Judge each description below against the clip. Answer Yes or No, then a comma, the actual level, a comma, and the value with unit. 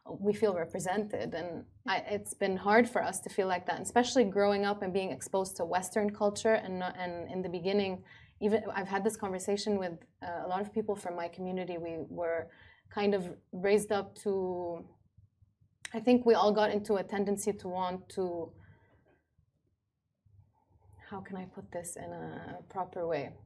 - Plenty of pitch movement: No, average, 3.2 semitones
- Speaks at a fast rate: Yes, fast, 180 wpm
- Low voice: No, high, 190 Hz